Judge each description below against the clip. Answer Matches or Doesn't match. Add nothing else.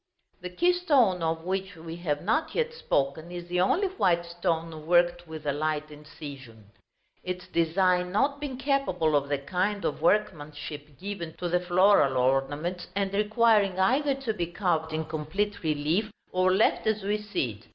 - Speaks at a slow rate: Doesn't match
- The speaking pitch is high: Doesn't match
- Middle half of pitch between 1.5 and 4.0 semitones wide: Doesn't match